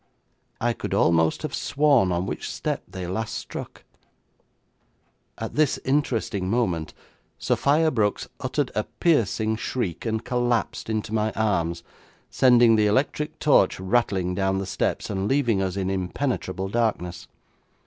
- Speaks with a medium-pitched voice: No, low, 110 Hz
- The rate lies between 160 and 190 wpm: No, slow, 135 wpm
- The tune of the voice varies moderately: Yes, average, 4.6 semitones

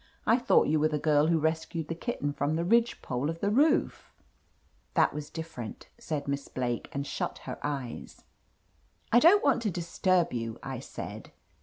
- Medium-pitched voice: Yes, medium, 160 Hz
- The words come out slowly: No, average, 185 wpm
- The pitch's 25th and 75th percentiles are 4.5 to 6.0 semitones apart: Yes, average, 4.8 semitones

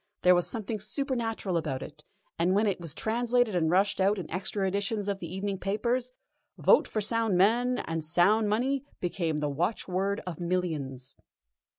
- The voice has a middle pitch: No, high, 195 Hz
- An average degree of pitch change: Yes, average, 4.2 semitones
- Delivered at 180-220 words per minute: No, average, 170 wpm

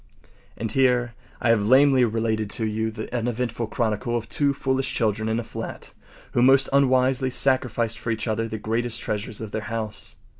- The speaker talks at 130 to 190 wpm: Yes, average, 180 wpm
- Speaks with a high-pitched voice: No, low, 115 Hz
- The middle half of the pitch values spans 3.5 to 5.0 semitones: No, average, 2.7 semitones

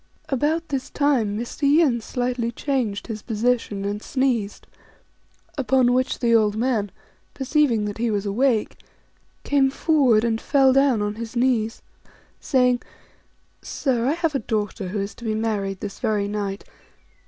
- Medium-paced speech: Yes, average, 155 wpm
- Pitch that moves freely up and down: No, average, 4.0 semitones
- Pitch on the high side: Yes, high, 235 Hz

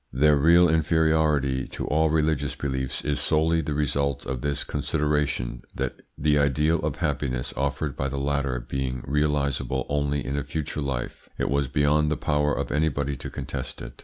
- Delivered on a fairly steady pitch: Yes, narrow, 1.9 semitones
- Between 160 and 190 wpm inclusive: Yes, average, 170 wpm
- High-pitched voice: No, very low, 70 Hz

